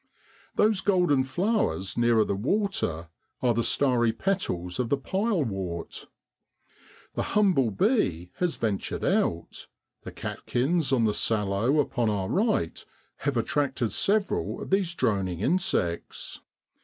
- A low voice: Yes, low, 125 Hz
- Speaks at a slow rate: Yes, slow, 120 wpm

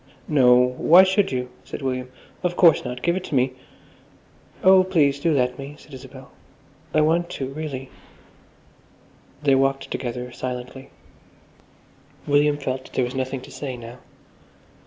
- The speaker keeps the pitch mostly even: No, average, 3.4 semitones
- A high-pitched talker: No, low, 135 Hz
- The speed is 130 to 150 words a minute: Yes, average, 145 wpm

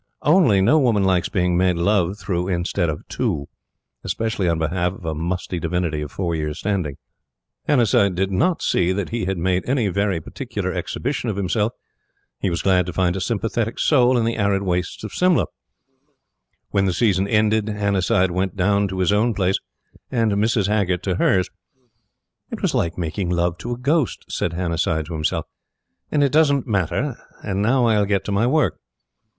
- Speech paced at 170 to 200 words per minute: Yes, average, 180 wpm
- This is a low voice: Yes, very low, 95 Hz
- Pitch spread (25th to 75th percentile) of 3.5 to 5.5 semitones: Yes, average, 3.8 semitones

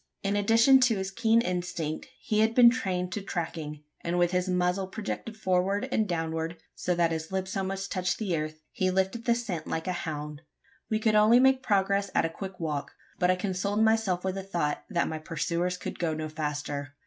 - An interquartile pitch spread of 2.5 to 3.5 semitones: No, average, 4.1 semitones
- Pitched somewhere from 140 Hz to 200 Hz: Yes, medium, 185 Hz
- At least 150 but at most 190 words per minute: No, fast, 205 wpm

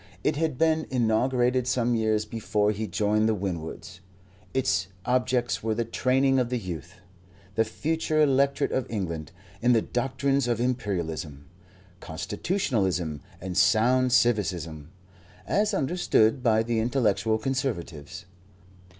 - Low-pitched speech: Yes, low, 115 Hz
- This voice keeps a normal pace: No, slow, 125 wpm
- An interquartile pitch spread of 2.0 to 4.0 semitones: No, average, 4.6 semitones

